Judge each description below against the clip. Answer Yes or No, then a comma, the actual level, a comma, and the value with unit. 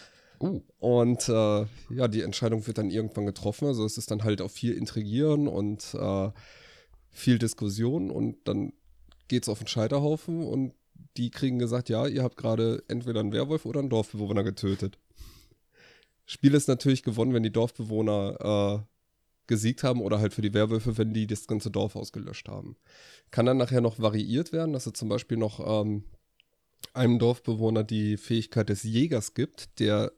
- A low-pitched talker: Yes, low, 110 Hz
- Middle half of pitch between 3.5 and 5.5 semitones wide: No, average, 2.9 semitones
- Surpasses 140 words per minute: Yes, average, 170 wpm